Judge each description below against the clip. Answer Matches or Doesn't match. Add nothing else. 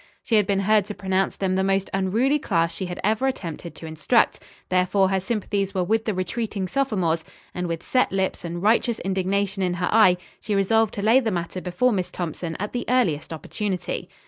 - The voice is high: Matches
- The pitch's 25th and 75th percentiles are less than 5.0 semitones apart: Matches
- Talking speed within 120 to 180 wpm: Doesn't match